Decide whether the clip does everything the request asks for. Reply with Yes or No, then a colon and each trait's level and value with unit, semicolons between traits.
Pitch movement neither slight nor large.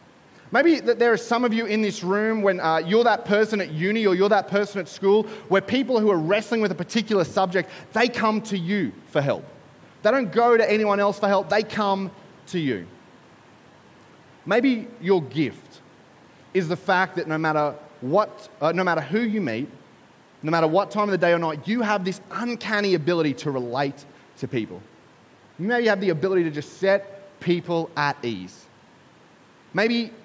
Yes: average, 4.2 semitones